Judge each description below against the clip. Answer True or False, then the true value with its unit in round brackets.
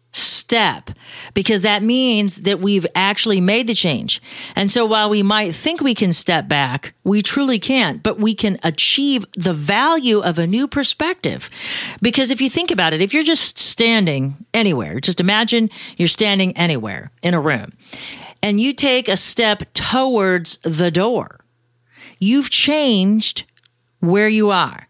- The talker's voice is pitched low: False (205 Hz)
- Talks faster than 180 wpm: False (155 wpm)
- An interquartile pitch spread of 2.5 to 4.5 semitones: False (5.2 semitones)